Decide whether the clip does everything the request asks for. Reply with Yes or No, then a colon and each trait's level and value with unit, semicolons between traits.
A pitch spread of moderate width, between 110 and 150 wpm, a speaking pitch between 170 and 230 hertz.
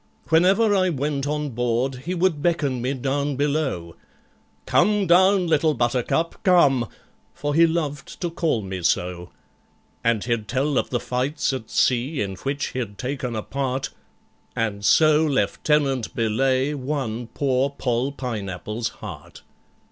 No: average, 4.2 semitones; average, 140 wpm; low, 135 Hz